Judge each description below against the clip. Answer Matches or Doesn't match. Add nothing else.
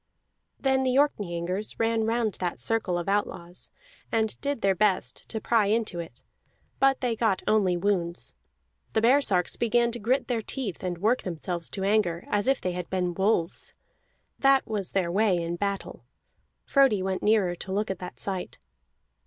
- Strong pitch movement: Doesn't match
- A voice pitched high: Matches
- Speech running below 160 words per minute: Doesn't match